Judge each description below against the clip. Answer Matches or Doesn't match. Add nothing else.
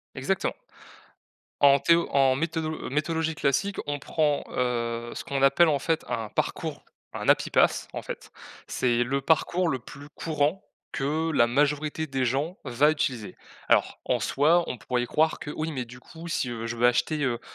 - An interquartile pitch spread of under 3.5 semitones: Doesn't match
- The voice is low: Doesn't match